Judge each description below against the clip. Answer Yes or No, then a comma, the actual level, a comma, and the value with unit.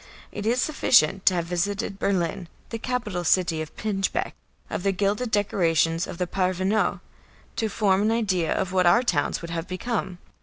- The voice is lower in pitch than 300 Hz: Yes, high, 190 Hz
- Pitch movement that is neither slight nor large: Yes, average, 3.3 semitones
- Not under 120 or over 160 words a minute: No, average, 175 wpm